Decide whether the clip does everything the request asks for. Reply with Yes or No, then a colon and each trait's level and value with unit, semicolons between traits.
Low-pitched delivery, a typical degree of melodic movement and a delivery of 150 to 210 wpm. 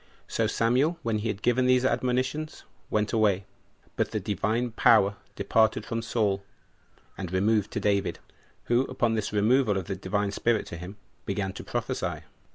Yes: low, 110 Hz; average, 3.2 semitones; average, 170 wpm